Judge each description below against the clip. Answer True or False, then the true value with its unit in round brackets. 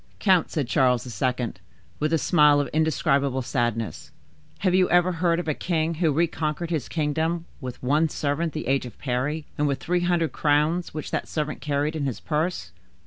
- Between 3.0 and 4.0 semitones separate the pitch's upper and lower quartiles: True (3.3 semitones)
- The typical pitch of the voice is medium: True (150 Hz)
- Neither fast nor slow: True (185 wpm)